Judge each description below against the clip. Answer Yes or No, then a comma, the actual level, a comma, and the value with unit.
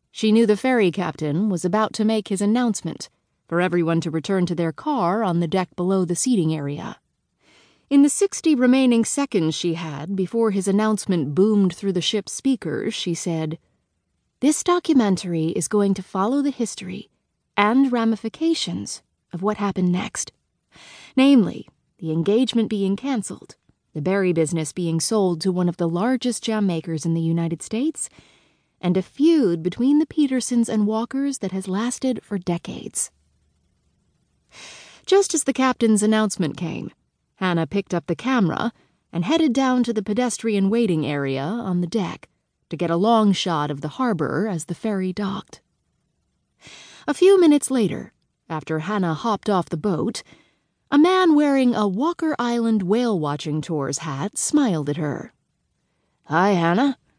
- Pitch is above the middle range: Yes, high, 200 Hz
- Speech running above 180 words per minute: No, average, 155 wpm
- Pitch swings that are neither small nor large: No, wide, 5.7 semitones